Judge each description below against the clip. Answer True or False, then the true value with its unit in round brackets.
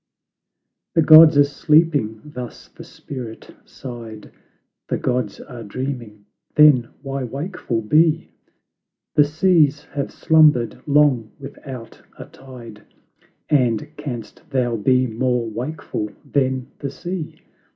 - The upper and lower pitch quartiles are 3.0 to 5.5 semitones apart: True (4.1 semitones)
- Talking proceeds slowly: True (110 wpm)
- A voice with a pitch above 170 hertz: False (130 Hz)